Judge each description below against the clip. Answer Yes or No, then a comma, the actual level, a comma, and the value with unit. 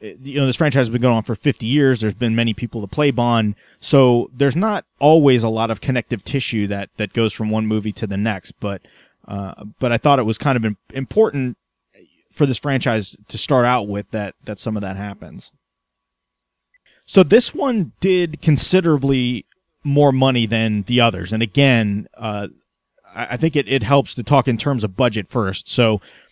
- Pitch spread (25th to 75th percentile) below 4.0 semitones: No, average, 4.5 semitones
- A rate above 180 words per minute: Yes, average, 195 wpm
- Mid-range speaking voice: No, low, 120 Hz